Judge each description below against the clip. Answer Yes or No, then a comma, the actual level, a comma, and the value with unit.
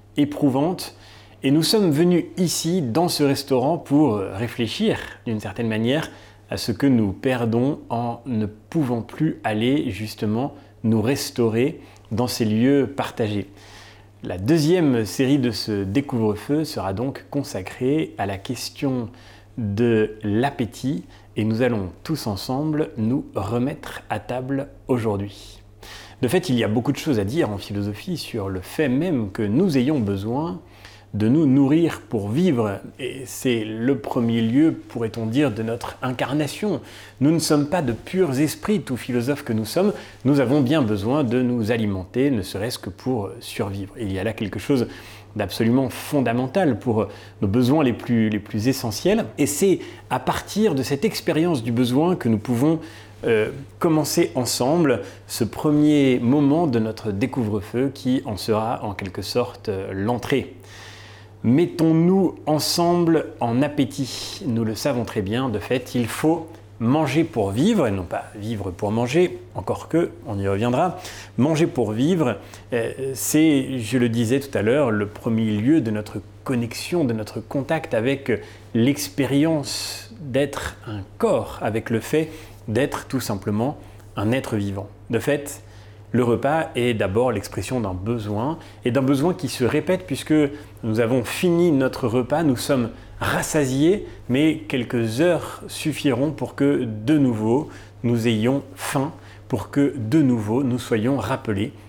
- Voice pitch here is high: No, low, 120 Hz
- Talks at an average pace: Yes, average, 155 wpm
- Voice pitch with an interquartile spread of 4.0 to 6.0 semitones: Yes, average, 4.8 semitones